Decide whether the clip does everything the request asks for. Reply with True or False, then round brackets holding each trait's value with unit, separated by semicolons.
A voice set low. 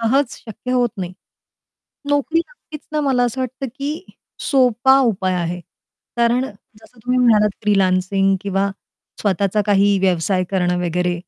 False (215 Hz)